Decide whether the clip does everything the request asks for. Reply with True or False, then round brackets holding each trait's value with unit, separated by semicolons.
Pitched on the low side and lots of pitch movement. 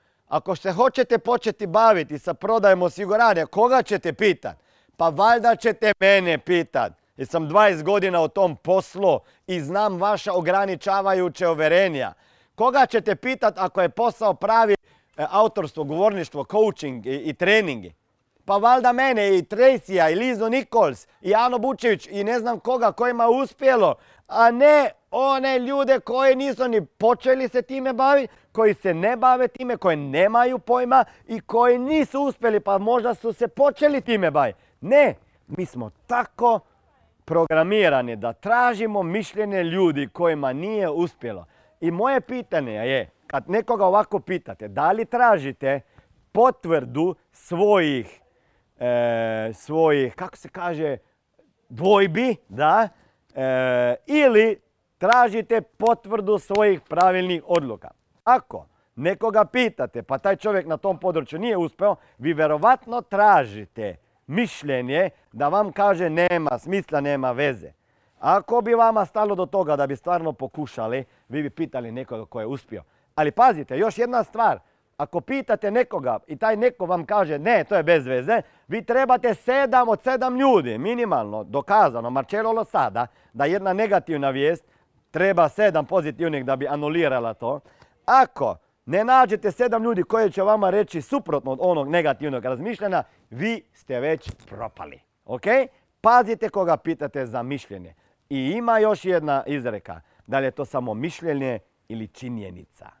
False (195 Hz; 7.6 semitones)